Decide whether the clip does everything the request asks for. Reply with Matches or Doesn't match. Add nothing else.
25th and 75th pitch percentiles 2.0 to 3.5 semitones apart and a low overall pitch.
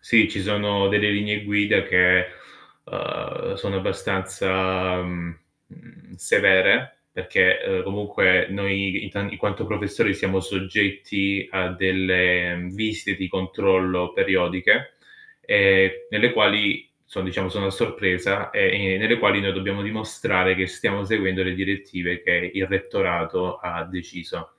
Doesn't match